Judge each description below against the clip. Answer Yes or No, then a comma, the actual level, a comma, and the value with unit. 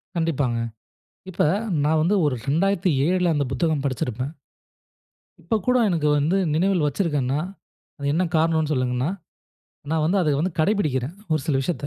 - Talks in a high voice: No, medium, 155 Hz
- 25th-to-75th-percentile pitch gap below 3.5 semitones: No, average, 3.8 semitones